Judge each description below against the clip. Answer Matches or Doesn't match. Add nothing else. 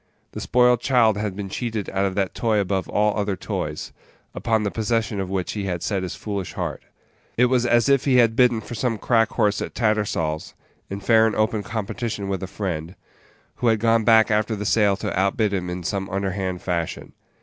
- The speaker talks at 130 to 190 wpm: Doesn't match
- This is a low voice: Matches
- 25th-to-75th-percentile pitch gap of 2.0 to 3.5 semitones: Matches